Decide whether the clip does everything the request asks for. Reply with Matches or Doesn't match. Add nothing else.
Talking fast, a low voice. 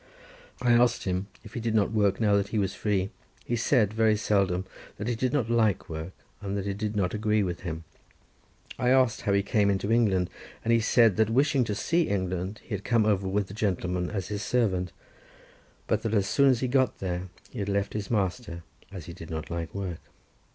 Matches